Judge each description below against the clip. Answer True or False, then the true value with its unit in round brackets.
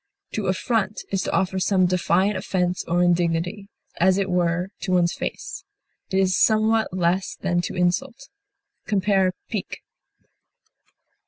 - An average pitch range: False (2.0 semitones)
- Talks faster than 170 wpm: False (135 wpm)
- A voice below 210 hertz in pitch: True (185 Hz)